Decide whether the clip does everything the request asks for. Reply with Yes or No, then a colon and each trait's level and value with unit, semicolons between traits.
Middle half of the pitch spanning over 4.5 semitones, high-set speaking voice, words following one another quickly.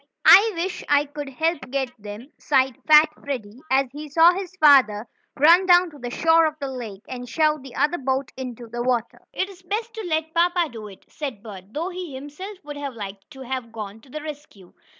Yes: average, 5.0 semitones; very high, 280 Hz; fast, 210 wpm